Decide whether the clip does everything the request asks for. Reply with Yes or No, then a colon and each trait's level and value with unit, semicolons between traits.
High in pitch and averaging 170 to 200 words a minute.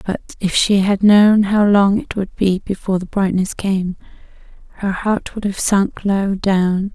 Yes: high, 195 Hz; average, 180 wpm